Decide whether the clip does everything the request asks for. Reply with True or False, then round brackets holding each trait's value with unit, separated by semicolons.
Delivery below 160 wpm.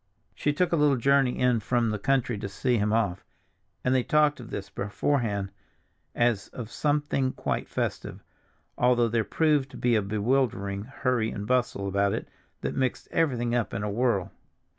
False (175 wpm)